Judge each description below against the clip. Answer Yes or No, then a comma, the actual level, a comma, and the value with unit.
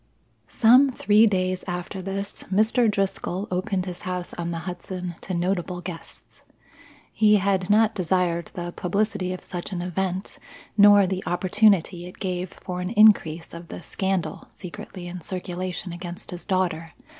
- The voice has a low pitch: No, medium, 185 Hz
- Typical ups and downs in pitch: No, narrow, 2.0 semitones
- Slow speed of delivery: No, average, 150 wpm